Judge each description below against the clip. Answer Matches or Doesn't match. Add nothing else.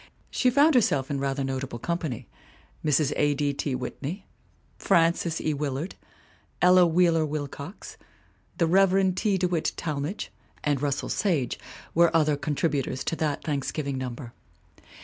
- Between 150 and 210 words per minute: Doesn't match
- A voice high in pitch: Doesn't match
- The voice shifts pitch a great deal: Doesn't match